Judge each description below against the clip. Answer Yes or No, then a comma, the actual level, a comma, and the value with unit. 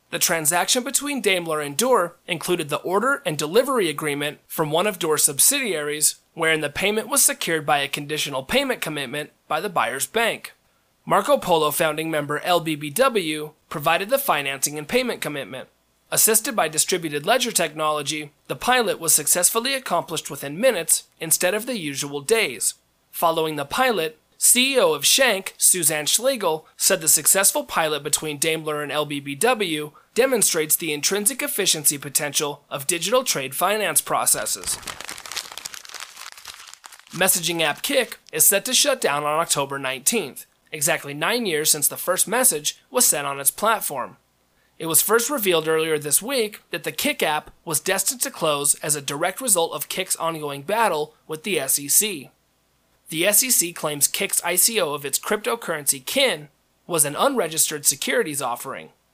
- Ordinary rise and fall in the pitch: No, wide, 6.4 semitones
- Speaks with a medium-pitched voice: Yes, medium, 165 Hz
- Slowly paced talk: No, average, 150 wpm